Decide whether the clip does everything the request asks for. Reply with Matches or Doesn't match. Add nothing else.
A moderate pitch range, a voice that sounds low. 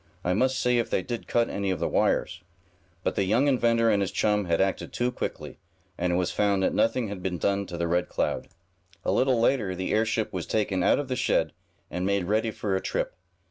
Matches